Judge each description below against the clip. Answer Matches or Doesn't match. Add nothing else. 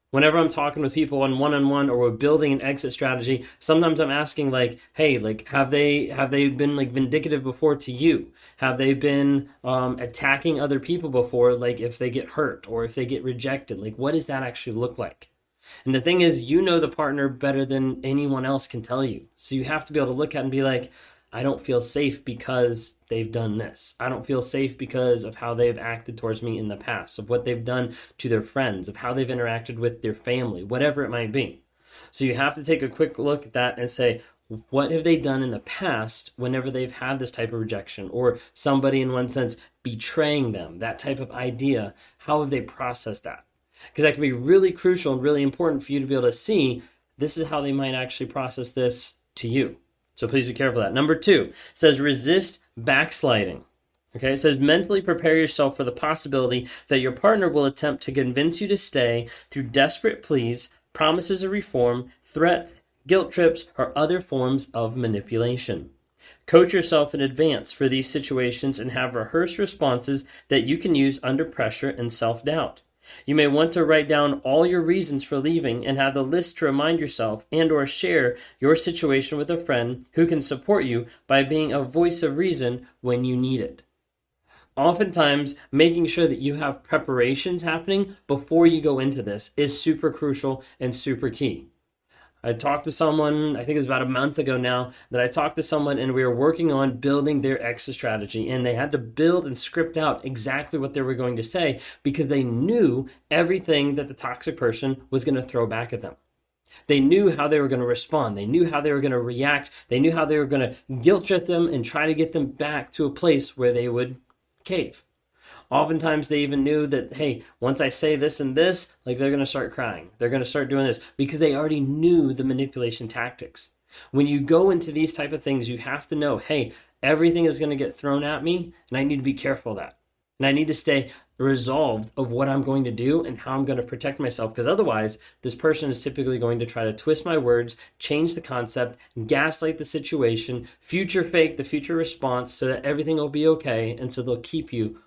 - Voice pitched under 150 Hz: Matches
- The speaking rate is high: Matches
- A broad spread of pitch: Doesn't match